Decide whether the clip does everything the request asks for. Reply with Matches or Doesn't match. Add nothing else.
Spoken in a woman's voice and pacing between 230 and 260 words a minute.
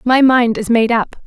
Matches